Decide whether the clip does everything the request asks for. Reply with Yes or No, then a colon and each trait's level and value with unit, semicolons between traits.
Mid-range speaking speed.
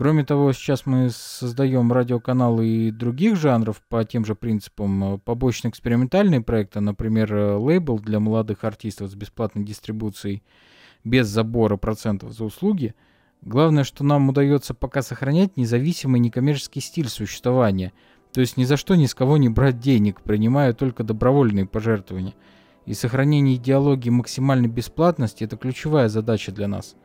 Yes: average, 140 wpm